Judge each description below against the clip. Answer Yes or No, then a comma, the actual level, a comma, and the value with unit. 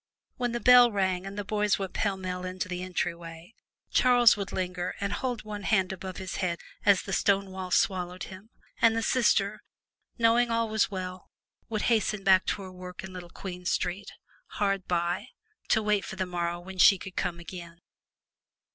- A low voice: No, high, 190 Hz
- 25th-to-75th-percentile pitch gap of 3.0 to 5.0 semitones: No, narrow, 2.5 semitones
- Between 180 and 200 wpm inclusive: Yes, average, 190 wpm